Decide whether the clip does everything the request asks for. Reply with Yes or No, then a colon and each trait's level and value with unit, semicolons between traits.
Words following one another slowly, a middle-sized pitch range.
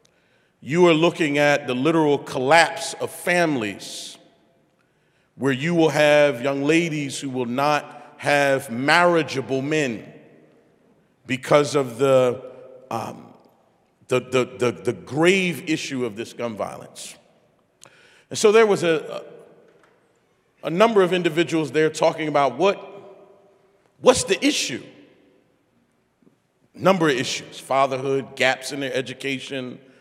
Yes: slow, 120 wpm; average, 4.6 semitones